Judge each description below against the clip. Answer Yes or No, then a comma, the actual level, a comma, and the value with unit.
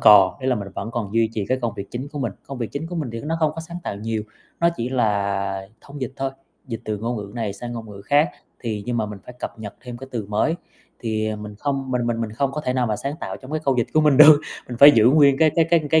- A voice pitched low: Yes, low, 120 Hz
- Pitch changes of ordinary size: Yes, average, 4.6 semitones